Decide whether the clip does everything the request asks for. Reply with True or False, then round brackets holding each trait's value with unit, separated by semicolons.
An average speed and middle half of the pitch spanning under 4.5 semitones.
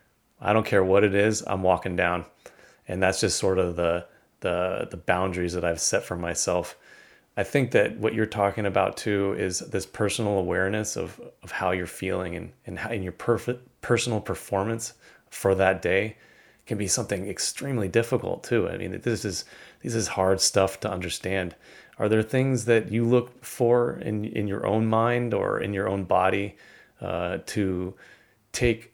True (180 wpm; 3.4 semitones)